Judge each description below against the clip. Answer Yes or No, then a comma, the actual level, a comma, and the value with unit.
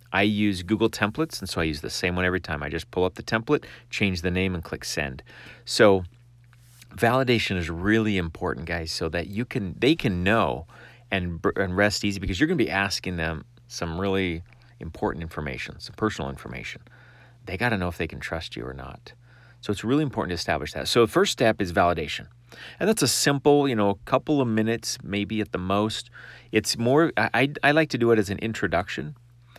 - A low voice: Yes, low, 105 Hz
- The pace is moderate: No, fast, 215 wpm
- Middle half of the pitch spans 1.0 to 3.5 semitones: No, average, 4.8 semitones